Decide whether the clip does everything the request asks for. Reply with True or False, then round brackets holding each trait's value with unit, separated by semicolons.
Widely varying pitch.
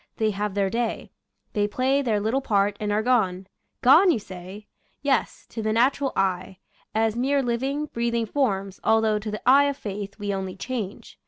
False (4.0 semitones)